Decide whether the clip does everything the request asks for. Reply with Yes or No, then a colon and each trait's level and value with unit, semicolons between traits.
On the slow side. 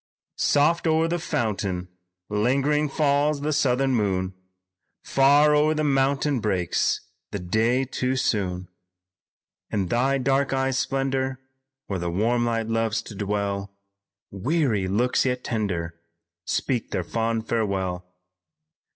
Yes: slow, 120 wpm